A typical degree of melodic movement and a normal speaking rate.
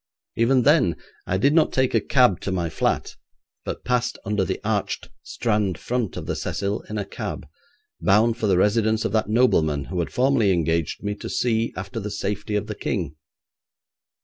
Yes: average, 3.7 semitones; average, 185 wpm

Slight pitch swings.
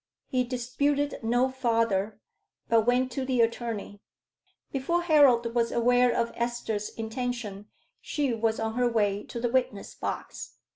Yes: narrow, 2.2 semitones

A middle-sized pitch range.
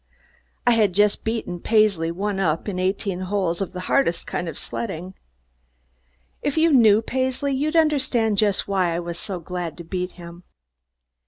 Yes: average, 4.2 semitones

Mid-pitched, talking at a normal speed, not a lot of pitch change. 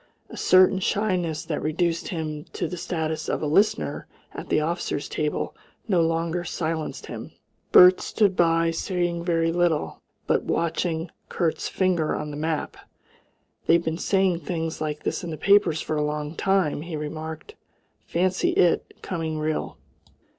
Yes: medium, 165 Hz; average, 155 wpm; narrow, 2.3 semitones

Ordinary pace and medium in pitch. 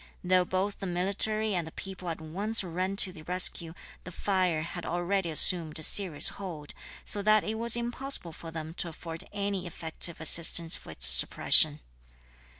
Yes: average, 170 wpm; medium, 180 Hz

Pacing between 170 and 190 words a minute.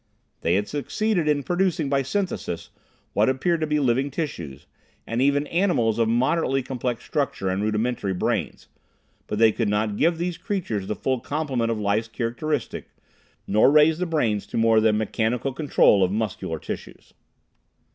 No: average, 160 wpm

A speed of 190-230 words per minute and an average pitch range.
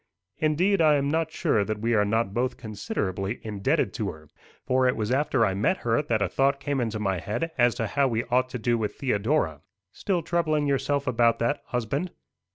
Yes: fast, 205 wpm; average, 4.9 semitones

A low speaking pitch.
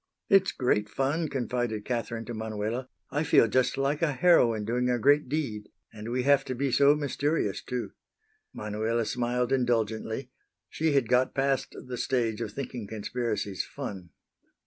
Yes: low, 125 Hz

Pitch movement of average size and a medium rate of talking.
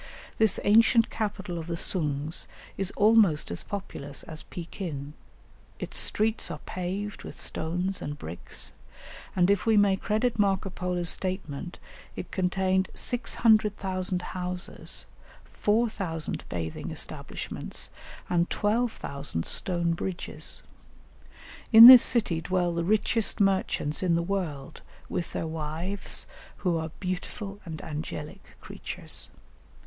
No: average, 3.9 semitones; slow, 115 wpm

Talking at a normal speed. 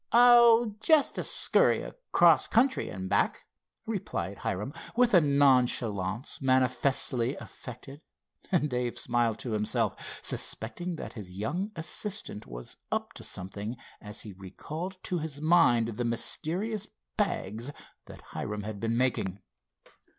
No: slow, 130 wpm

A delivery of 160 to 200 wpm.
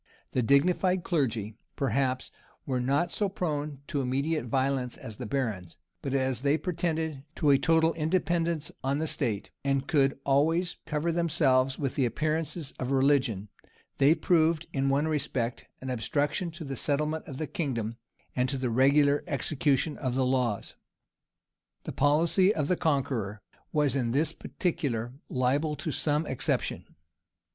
No: average, 150 wpm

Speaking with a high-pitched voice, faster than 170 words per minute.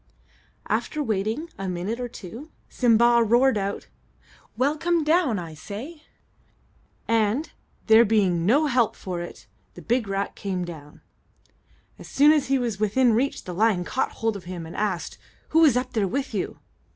No: high, 225 Hz; average, 165 wpm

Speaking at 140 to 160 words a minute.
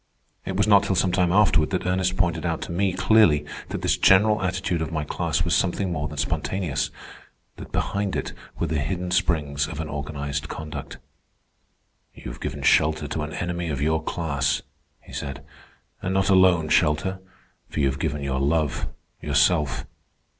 No: average, 175 wpm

